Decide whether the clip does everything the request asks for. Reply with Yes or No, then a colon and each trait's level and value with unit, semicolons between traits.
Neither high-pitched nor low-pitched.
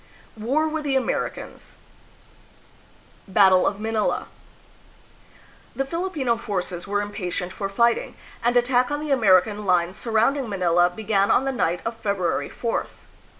No: high, 220 Hz